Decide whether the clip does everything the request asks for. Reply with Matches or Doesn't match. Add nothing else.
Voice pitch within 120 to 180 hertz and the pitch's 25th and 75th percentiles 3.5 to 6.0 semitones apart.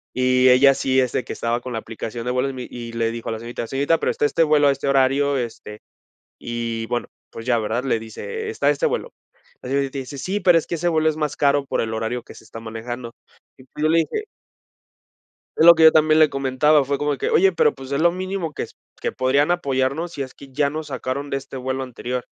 Matches